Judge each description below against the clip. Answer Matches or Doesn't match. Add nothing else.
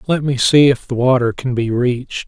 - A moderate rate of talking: Doesn't match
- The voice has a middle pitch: Doesn't match